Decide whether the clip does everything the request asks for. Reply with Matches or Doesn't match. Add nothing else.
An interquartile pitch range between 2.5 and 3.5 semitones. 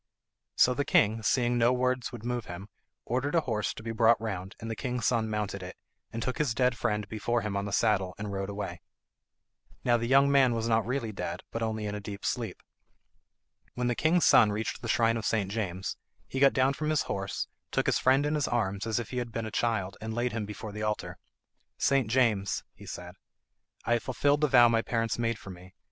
Matches